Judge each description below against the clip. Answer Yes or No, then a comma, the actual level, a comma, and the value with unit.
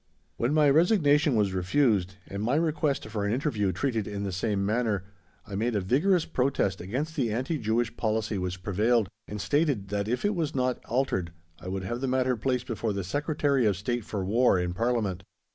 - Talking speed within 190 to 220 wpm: Yes, average, 195 wpm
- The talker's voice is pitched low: Yes, low, 115 Hz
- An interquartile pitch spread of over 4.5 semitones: Yes, average, 5.3 semitones